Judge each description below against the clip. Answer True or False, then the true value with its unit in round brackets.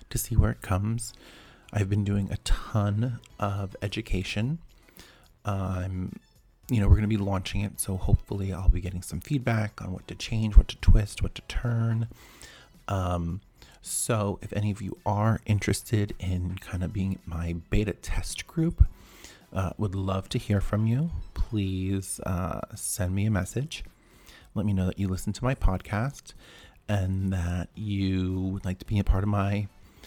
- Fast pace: False (170 wpm)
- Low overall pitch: True (100 Hz)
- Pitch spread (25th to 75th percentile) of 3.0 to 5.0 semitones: False (2.5 semitones)